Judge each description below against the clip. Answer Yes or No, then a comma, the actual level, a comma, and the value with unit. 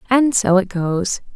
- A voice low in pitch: No, high, 205 Hz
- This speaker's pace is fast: No, average, 175 wpm